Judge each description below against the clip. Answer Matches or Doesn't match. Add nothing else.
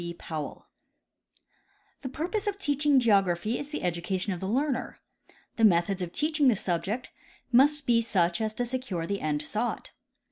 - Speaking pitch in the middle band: Doesn't match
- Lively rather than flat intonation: Matches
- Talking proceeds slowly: Doesn't match